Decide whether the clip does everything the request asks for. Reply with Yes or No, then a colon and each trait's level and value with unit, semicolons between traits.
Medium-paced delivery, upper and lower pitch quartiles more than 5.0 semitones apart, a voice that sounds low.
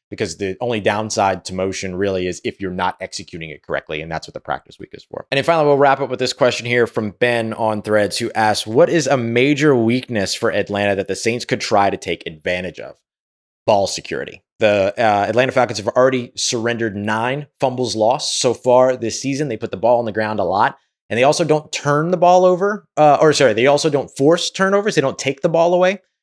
No: fast, 230 wpm; wide, 5.4 semitones; low, 120 Hz